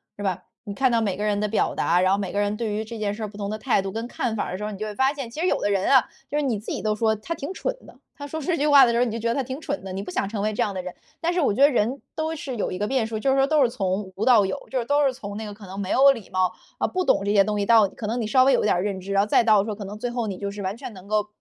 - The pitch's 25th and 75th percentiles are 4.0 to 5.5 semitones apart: Yes, average, 4.4 semitones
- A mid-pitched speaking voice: No, high, 215 Hz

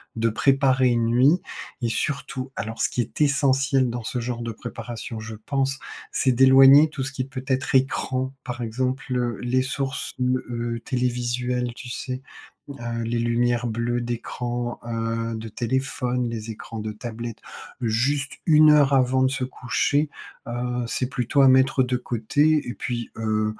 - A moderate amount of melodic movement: No, narrow, 2.1 semitones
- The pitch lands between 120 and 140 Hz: Yes, low, 125 Hz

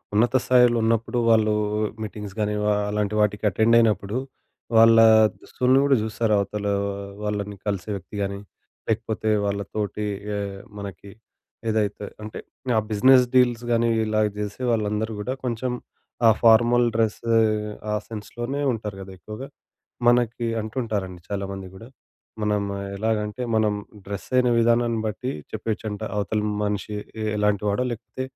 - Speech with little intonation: Yes, narrow, 2.3 semitones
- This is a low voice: Yes, low, 110 Hz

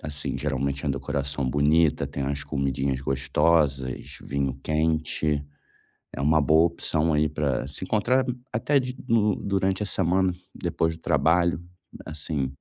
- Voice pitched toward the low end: Yes, very low, 75 Hz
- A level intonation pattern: No, average, 3.5 semitones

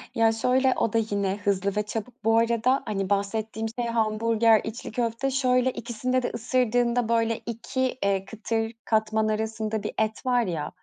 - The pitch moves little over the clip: Yes, narrow, 2.0 semitones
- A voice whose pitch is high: Yes, high, 225 Hz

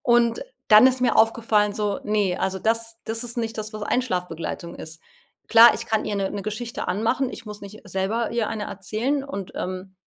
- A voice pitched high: Yes, high, 215 Hz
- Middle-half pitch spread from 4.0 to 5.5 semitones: No, average, 2.7 semitones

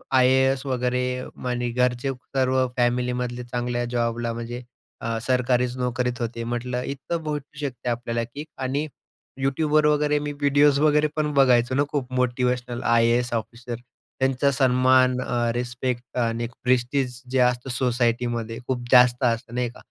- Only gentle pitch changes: Yes, narrow, 1.6 semitones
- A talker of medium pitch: No, low, 125 Hz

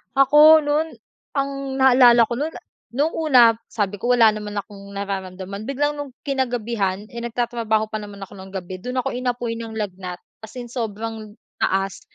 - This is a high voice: Yes, high, 230 Hz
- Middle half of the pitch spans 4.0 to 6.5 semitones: Yes, average, 4.3 semitones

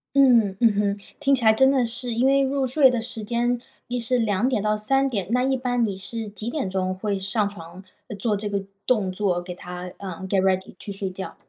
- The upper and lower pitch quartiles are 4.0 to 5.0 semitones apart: Yes, average, 4.3 semitones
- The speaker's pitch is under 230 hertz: Yes, high, 215 Hz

